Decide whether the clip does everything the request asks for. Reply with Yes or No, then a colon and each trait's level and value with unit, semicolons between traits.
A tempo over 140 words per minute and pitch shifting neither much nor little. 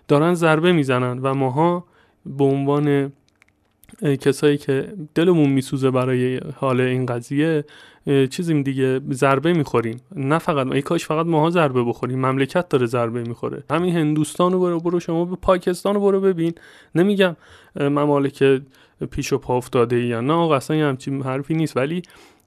Yes: average, 150 wpm; average, 4.0 semitones